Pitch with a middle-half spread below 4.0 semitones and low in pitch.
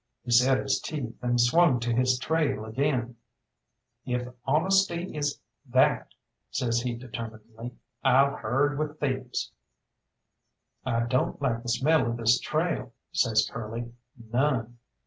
Yes: average, 3.5 semitones; low, 125 Hz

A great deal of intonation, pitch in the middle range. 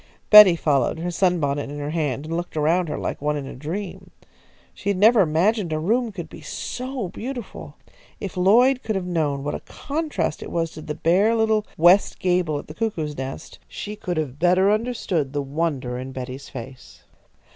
Yes: wide, 5.8 semitones; medium, 170 Hz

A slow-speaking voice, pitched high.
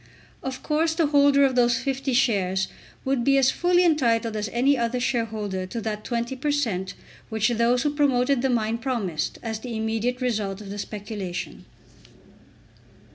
No: average, 165 wpm; high, 240 Hz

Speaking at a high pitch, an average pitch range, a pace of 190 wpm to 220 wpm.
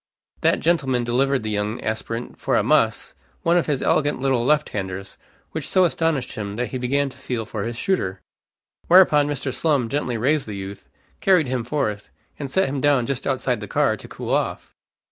No: low, 130 Hz; average, 4.4 semitones; average, 195 wpm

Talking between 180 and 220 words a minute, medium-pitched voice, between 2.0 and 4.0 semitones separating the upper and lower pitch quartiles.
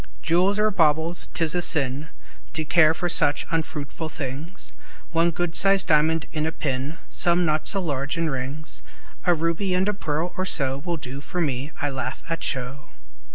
Yes: average, 185 wpm; medium, 160 Hz; average, 3.2 semitones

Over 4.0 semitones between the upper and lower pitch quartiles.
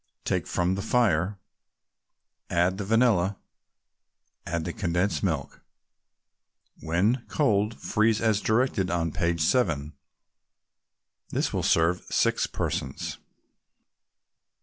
Yes: average, 4.4 semitones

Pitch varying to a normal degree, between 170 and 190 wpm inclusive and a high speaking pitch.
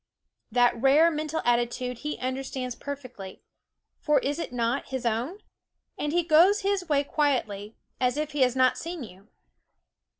No: average, 4.0 semitones; average, 155 wpm; very high, 270 Hz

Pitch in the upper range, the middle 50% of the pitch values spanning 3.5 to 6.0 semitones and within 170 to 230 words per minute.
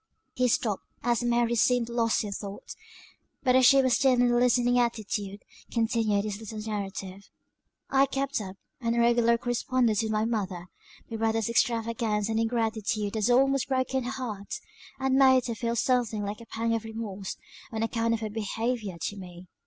No: high, 230 Hz; narrow, 2.4 semitones; average, 175 wpm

